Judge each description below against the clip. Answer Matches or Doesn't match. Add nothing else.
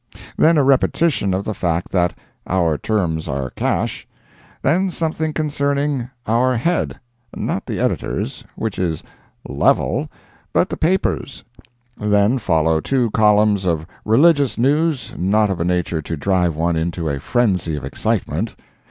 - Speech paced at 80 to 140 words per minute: Matches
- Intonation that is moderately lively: Doesn't match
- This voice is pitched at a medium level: Doesn't match